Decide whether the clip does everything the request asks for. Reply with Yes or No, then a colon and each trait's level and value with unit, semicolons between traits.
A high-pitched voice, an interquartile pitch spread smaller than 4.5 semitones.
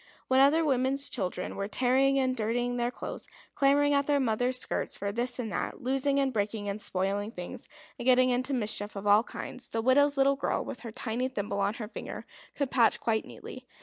Yes: high, 245 Hz; average, 4.0 semitones